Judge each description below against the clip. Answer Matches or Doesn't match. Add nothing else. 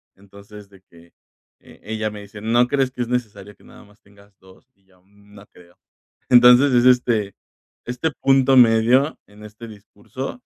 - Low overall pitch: Matches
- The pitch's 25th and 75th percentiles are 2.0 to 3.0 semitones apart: Doesn't match